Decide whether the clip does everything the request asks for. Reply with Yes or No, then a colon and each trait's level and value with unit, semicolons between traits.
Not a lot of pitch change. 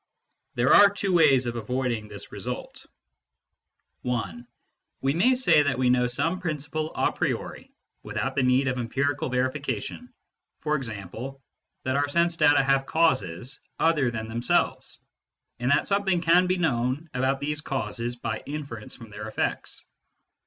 No: average, 4.4 semitones